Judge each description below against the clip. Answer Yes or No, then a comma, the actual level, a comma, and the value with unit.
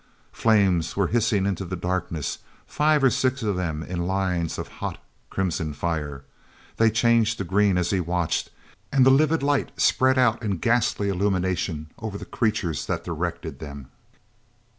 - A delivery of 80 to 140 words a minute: No, average, 160 wpm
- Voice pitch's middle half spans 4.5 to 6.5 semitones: Yes, average, 5.1 semitones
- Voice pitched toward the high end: No, very low, 95 Hz